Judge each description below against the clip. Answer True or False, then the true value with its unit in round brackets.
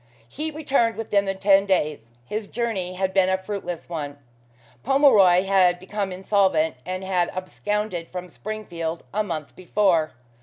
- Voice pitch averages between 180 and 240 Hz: True (190 Hz)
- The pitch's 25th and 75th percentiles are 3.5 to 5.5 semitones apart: False (2.9 semitones)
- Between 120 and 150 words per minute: True (145 wpm)